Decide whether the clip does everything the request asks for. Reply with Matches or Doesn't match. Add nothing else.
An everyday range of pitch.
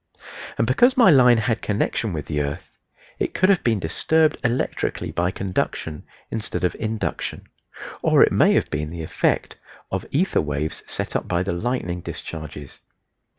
Doesn't match